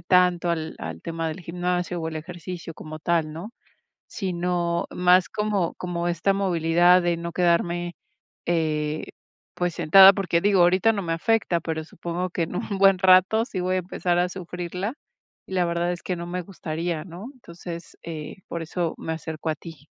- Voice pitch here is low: No, medium, 175 Hz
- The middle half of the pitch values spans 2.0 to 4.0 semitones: No, narrow, 1.6 semitones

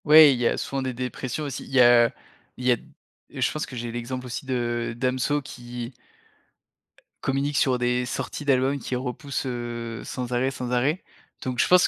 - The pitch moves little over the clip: Yes, narrow, 1.9 semitones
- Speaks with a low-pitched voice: Yes, low, 125 Hz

